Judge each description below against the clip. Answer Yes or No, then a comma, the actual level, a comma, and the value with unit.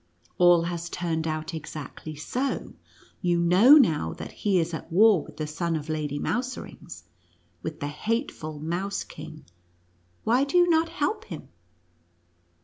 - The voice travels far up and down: Yes, wide, 6.5 semitones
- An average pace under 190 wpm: Yes, average, 150 wpm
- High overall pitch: No, medium, 170 Hz